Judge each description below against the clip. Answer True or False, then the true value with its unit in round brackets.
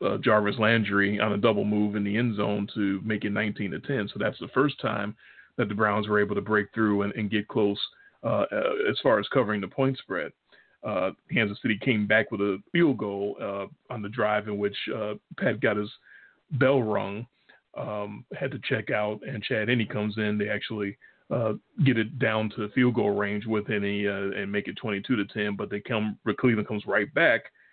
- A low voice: True (105 Hz)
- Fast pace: True (220 wpm)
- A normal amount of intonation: False (1.2 semitones)